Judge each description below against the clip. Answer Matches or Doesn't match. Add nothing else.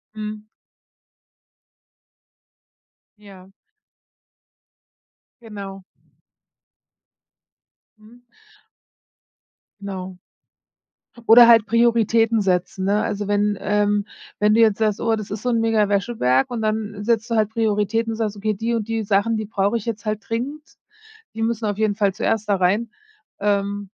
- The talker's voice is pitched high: Matches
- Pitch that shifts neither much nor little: Doesn't match